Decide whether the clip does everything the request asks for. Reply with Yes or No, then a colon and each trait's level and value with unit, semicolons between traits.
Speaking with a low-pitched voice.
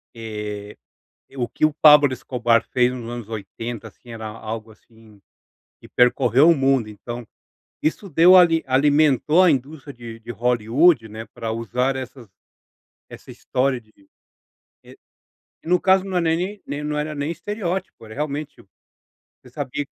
Yes: low, 130 Hz